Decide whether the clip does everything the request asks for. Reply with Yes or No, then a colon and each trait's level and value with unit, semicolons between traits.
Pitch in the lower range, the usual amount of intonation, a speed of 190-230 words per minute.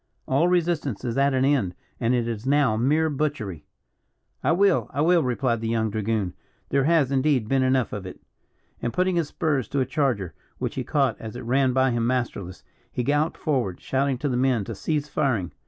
Yes: low, 130 Hz; average, 4.1 semitones; fast, 205 wpm